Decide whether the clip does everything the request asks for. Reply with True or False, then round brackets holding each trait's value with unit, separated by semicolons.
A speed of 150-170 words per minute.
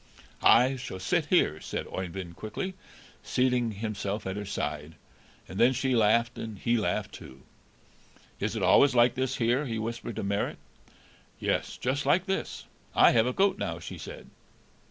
True (165 wpm)